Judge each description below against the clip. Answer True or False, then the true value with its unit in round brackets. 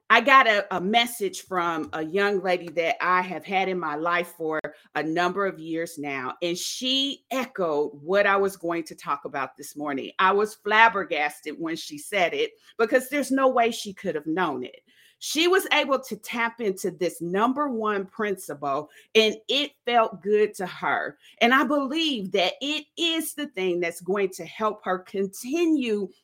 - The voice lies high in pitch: True (195 Hz)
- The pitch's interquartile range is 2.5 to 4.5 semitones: False (5.6 semitones)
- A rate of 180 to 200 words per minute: True (185 wpm)